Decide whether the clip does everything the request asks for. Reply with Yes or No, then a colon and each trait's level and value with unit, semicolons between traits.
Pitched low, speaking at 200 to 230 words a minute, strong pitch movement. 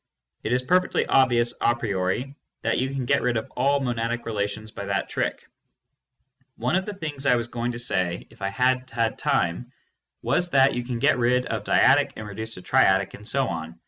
No: low, 120 Hz; fast, 205 wpm; average, 3.5 semitones